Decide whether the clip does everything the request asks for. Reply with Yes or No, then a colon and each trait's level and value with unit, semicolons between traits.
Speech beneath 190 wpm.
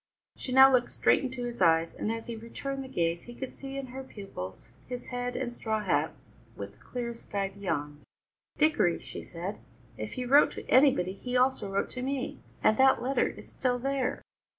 No: average, 200 wpm